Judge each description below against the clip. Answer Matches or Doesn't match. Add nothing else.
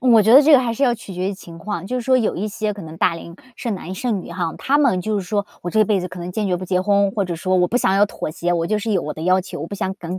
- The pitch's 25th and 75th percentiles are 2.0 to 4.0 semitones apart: Matches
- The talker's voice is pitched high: Matches